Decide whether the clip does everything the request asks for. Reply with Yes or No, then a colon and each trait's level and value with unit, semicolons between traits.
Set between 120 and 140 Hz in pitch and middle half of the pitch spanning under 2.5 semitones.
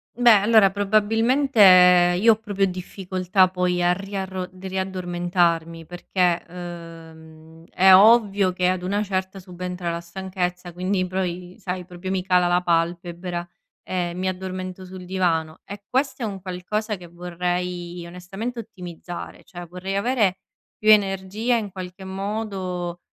No: medium, 185 Hz; narrow, 1.8 semitones